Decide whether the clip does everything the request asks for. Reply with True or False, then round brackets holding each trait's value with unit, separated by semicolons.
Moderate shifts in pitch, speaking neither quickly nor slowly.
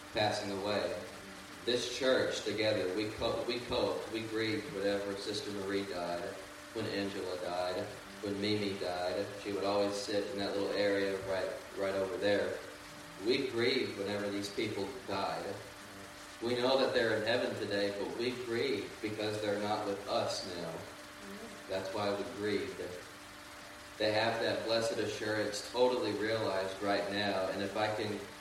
False (1.3 semitones; 150 wpm)